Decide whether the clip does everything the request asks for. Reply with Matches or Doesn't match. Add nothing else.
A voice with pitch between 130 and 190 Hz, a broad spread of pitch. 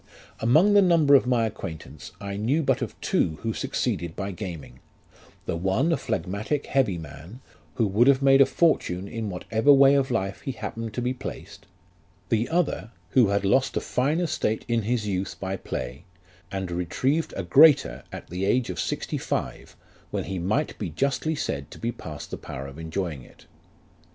Doesn't match